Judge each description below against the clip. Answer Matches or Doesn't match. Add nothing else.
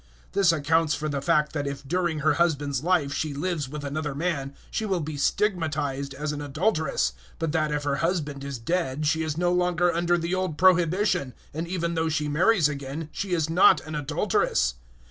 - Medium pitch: Matches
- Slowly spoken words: Doesn't match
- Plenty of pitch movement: Doesn't match